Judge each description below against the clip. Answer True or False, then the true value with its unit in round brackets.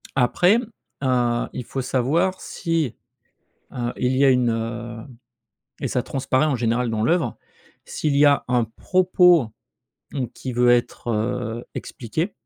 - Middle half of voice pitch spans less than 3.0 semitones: False (3.8 semitones)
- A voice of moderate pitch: False (125 Hz)